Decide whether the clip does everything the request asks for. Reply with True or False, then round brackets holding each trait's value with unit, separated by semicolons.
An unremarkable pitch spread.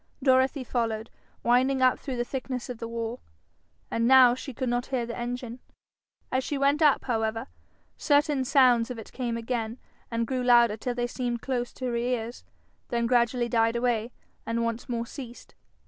False (1.8 semitones)